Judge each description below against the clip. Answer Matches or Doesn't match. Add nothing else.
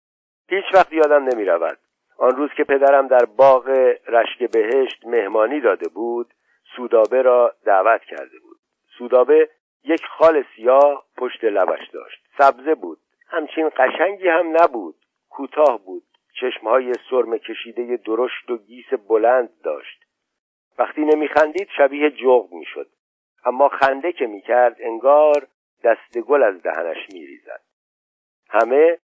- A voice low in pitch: Doesn't match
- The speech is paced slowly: Doesn't match